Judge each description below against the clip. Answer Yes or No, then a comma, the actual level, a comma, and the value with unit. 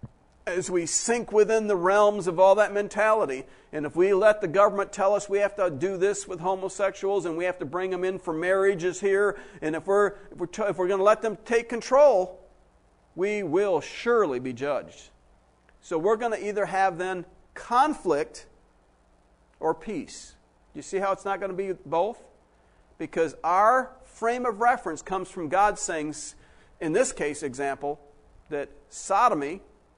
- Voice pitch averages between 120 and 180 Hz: No, high, 190 Hz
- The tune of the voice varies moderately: Yes, average, 4.0 semitones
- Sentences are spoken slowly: No, average, 175 wpm